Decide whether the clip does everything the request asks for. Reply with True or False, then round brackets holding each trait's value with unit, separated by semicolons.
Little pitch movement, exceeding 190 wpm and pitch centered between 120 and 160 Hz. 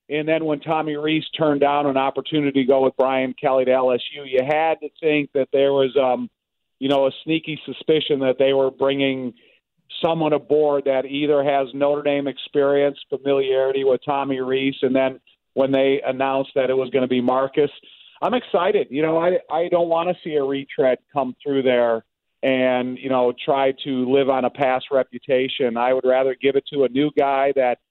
True (1.9 semitones; 200 wpm; 135 Hz)